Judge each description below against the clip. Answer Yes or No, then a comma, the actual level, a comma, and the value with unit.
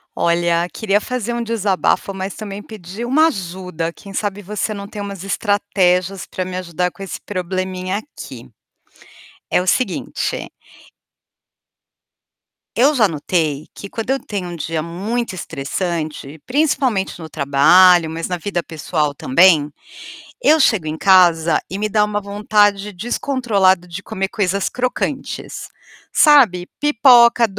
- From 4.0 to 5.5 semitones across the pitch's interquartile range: No, average, 3.6 semitones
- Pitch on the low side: No, high, 190 Hz